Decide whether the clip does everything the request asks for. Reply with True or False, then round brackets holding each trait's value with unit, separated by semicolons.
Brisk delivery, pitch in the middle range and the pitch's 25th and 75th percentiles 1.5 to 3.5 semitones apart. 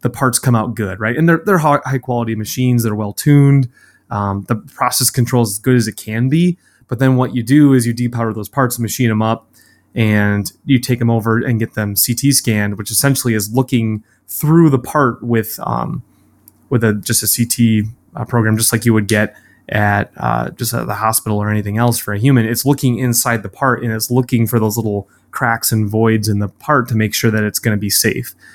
False (225 wpm; 115 Hz; 2.8 semitones)